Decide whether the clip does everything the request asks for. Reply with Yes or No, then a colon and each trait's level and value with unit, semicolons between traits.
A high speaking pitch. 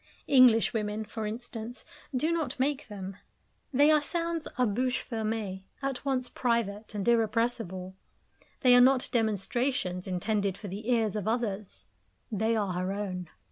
Yes: high, 225 Hz